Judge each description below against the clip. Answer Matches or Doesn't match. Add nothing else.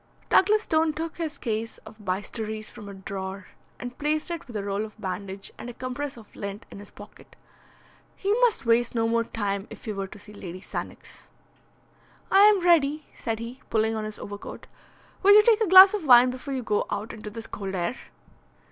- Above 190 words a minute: Matches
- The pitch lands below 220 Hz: Doesn't match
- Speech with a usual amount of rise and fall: Doesn't match